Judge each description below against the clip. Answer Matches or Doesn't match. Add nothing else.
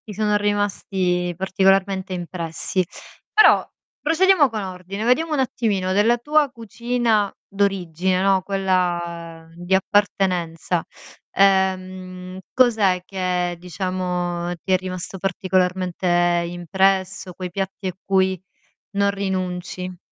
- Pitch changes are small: Matches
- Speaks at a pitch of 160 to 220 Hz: Matches